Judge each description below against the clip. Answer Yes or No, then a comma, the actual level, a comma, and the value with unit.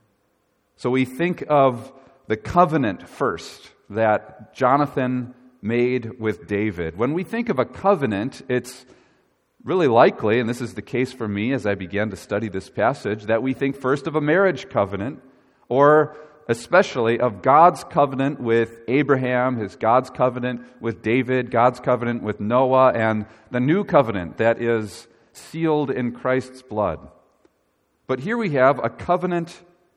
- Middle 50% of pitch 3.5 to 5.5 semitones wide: Yes, average, 3.8 semitones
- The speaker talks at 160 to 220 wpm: No, average, 150 wpm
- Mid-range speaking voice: No, low, 125 Hz